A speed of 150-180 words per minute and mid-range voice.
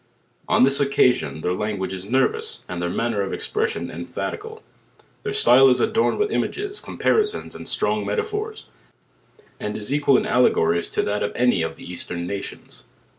No: average, 175 wpm; low, 125 Hz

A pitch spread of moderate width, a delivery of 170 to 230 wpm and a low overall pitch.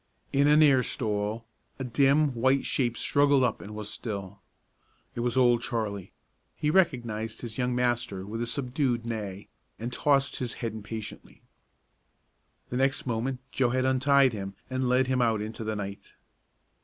No: average, 3.2 semitones; average, 160 wpm; low, 120 Hz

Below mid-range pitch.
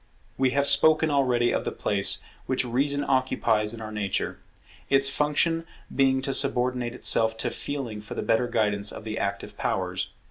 Yes: low, 125 Hz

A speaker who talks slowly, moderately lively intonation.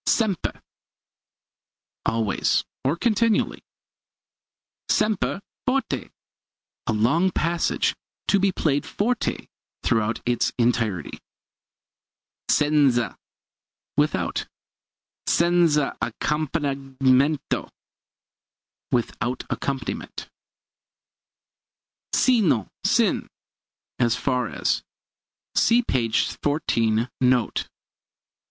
No: slow, 65 wpm; wide, 6.4 semitones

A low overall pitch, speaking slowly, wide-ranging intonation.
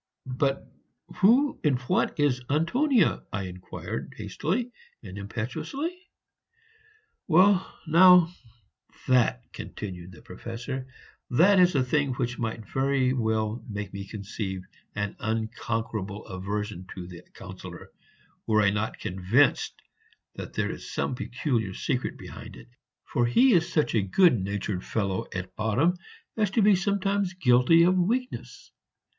Yes: low, 125 Hz; slow, 130 wpm; wide, 9.0 semitones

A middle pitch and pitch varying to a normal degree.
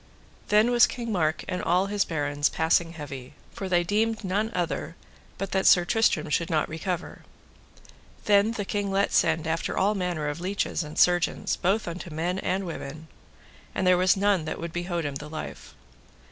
Yes: medium, 180 Hz; average, 3.7 semitones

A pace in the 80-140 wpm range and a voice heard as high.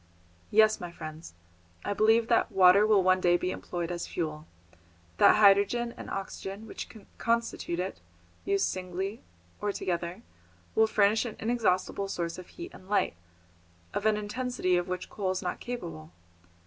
No: average, 155 wpm; high, 195 Hz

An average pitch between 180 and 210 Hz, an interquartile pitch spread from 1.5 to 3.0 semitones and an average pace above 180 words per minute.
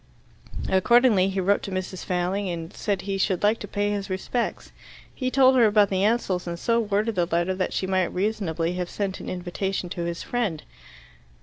Yes: high, 190 Hz; narrow, 2.6 semitones; average, 195 wpm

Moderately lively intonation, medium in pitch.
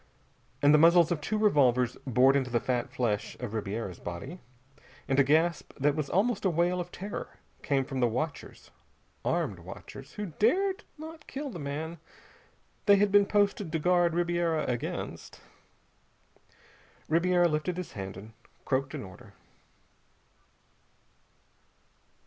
No: wide, 5.8 semitones; medium, 160 Hz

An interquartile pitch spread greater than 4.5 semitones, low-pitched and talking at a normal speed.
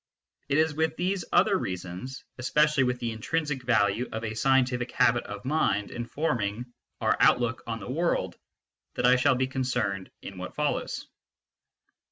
Yes: average, 4.9 semitones; low, 125 Hz; average, 165 wpm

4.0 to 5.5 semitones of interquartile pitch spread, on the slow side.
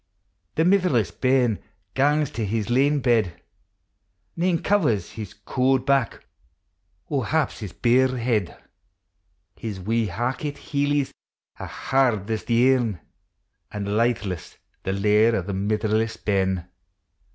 Yes: average, 4.3 semitones; slow, 125 wpm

